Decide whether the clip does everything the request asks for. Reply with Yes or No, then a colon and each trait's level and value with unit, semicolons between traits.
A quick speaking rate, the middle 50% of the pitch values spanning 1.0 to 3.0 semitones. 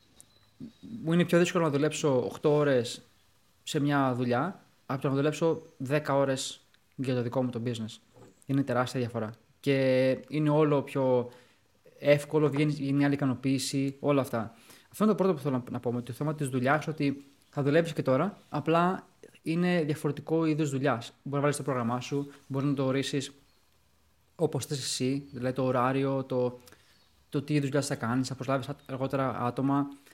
Yes: fast, 175 wpm; narrow, 2.6 semitones